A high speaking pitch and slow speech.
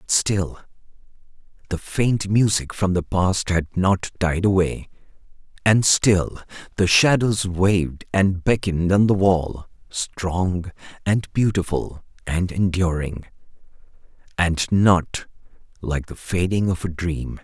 No: very low, 90 Hz; slow, 120 wpm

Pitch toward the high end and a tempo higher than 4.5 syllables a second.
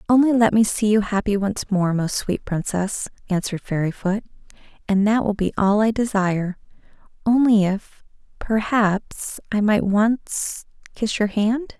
No: high, 210 Hz; 4.3 syllables/s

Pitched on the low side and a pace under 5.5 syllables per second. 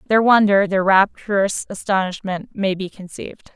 No: high, 195 Hz; 4.9 syllables/s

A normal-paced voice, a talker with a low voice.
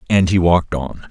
No: fast, 220 wpm; very low, 85 Hz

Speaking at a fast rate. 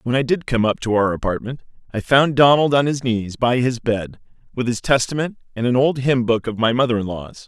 Yes: fast, 240 wpm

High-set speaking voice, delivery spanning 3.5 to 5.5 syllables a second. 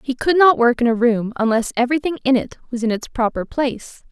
No: very high, 250 Hz; 6.0 syllables/s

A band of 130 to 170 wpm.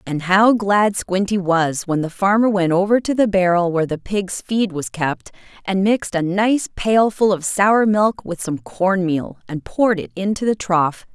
No: average, 200 wpm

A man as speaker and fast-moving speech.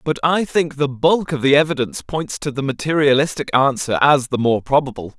No: male; average, 195 wpm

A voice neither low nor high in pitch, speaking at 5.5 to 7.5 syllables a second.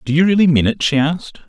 Yes: medium, 155 Hz; 6.8 syllables/s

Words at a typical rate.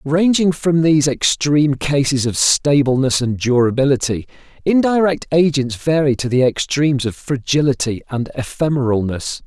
No: slow, 120 wpm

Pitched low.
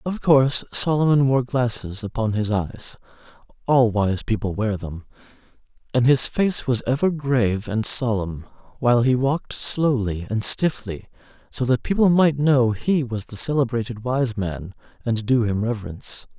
Yes: low, 120 Hz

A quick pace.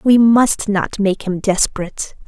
No: average, 160 wpm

